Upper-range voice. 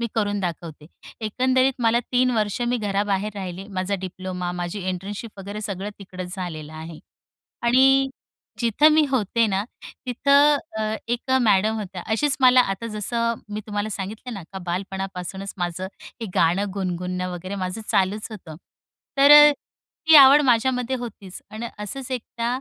Yes: high, 205 Hz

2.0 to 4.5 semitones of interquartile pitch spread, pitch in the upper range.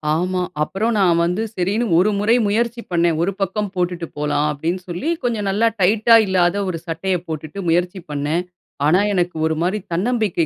No: average, 3.4 semitones; medium, 180 Hz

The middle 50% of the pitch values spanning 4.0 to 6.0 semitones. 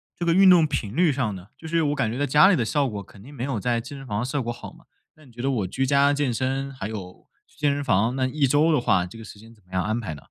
Yes: average, 4.8 semitones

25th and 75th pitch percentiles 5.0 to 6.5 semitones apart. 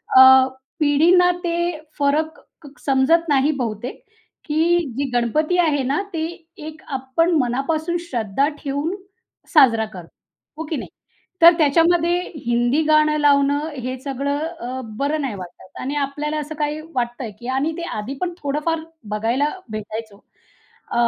No: average, 3.6 semitones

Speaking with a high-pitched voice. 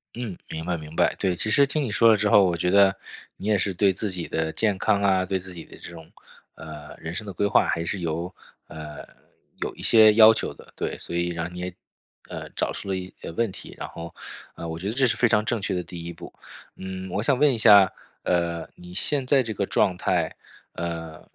No: very low, 95 Hz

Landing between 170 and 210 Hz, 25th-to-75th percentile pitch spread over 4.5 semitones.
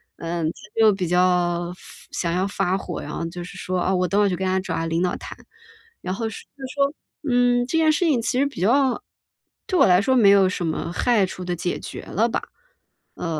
Yes: high, 190 Hz; average, 5.2 semitones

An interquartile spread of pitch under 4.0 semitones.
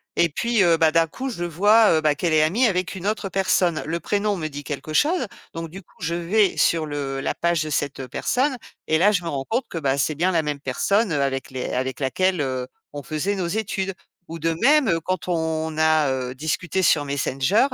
No: average, 4.8 semitones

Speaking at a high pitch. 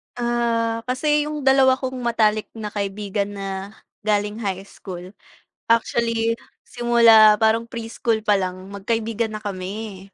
Yes: high, 220 Hz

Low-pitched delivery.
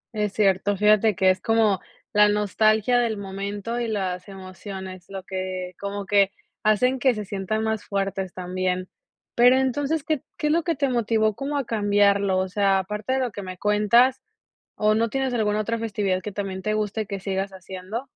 No: high, 205 Hz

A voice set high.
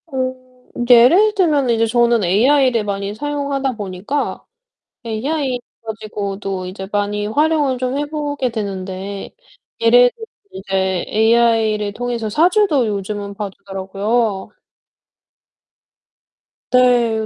Yes: high, 230 Hz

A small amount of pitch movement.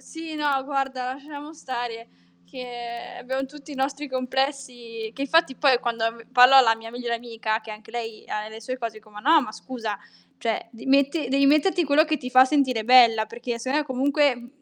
No: average, 3.2 semitones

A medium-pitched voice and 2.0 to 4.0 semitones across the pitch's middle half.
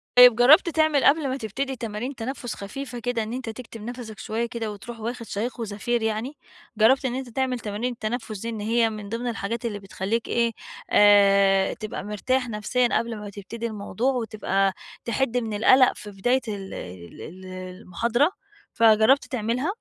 No: high, 230 Hz; average, 3.1 semitones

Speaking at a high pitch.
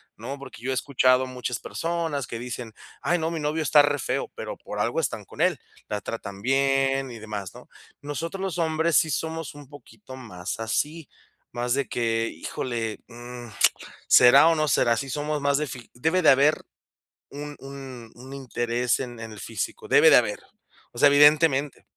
No: low, 135 Hz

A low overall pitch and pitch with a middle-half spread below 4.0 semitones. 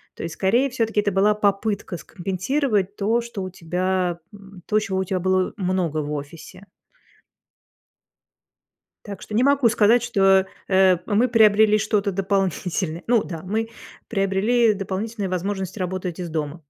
No: high, 195 Hz; narrow, 2.6 semitones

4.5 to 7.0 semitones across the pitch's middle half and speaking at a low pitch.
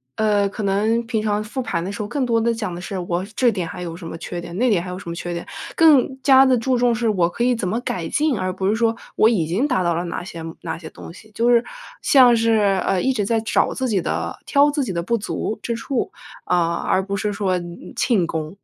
No: average, 4.8 semitones; high, 210 Hz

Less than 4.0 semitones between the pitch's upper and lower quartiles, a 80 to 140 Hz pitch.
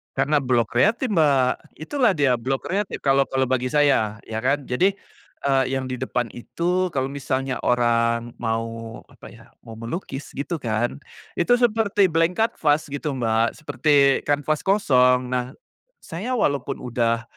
No: average, 4.4 semitones; low, 135 Hz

